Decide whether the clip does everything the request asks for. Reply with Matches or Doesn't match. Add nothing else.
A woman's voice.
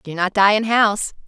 Matches